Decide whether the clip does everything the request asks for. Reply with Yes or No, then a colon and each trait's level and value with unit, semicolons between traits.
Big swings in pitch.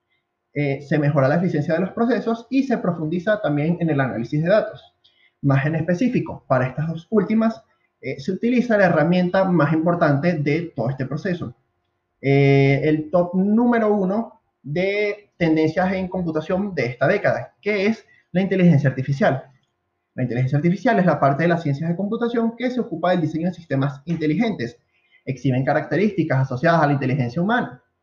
Yes: wide, 5.9 semitones